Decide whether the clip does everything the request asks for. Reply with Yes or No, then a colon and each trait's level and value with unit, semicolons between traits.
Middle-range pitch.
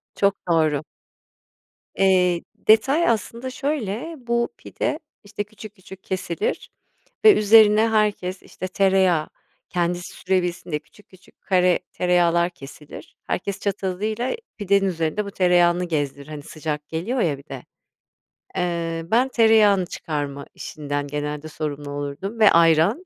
Yes: medium, 180 Hz